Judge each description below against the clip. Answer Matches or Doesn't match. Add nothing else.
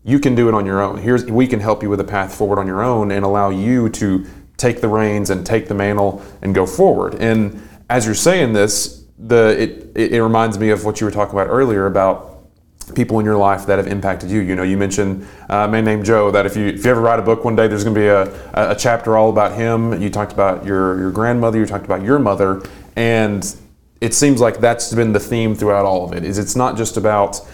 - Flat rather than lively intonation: Matches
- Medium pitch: Doesn't match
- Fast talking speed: Matches